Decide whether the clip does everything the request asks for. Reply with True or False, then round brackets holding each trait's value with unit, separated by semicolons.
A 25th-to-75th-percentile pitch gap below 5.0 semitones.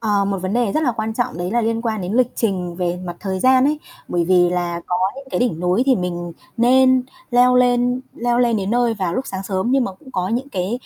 False (5.3 semitones)